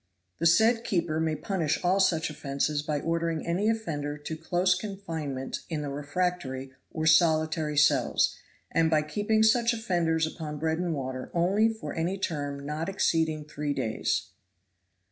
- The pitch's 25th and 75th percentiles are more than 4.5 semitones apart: No, average, 3.2 semitones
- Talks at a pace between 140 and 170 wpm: Yes, average, 150 wpm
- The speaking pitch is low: No, medium, 160 Hz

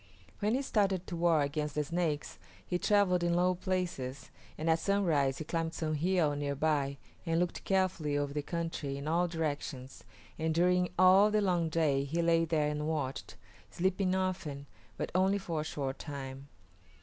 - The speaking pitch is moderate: Yes, medium, 165 Hz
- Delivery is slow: No, average, 175 wpm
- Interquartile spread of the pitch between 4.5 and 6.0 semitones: No, average, 3.7 semitones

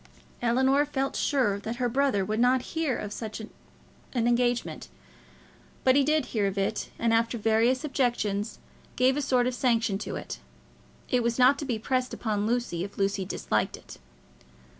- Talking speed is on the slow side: No, average, 170 wpm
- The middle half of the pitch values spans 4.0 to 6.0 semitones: No, average, 3.3 semitones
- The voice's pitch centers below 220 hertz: No, high, 240 Hz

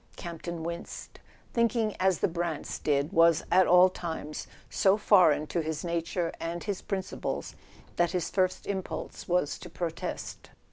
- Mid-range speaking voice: Yes, medium, 175 Hz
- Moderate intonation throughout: No, narrow, 2.2 semitones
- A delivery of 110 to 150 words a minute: Yes, average, 145 wpm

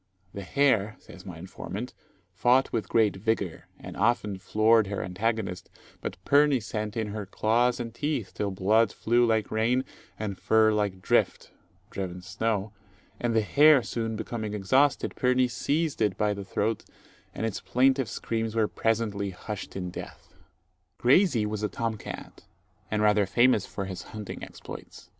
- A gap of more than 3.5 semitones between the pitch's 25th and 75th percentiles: No, average, 2.9 semitones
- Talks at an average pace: Yes, average, 155 wpm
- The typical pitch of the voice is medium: No, low, 110 Hz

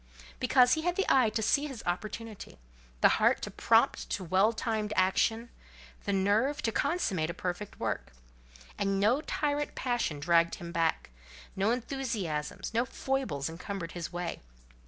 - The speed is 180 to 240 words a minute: No, average, 155 wpm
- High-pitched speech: Yes, high, 210 Hz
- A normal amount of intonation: No, wide, 6.1 semitones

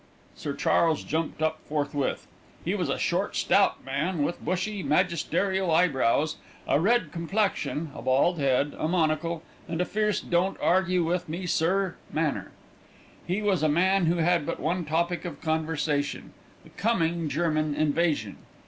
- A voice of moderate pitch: Yes, medium, 165 Hz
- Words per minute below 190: Yes, average, 150 wpm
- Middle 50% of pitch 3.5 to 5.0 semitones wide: No, average, 2.9 semitones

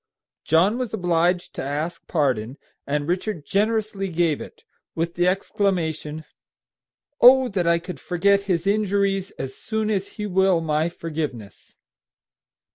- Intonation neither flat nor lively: Yes, average, 3.9 semitones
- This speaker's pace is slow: Yes, slow, 130 wpm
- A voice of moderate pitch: Yes, medium, 175 Hz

